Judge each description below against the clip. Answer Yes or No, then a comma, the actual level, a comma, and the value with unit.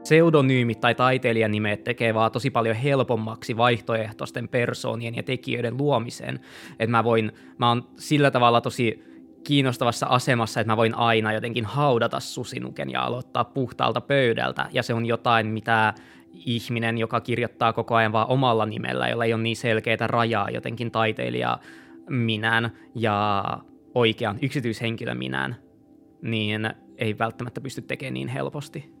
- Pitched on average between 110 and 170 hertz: Yes, low, 115 Hz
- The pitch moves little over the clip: Yes, narrow, 1.9 semitones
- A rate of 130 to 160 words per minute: Yes, average, 140 wpm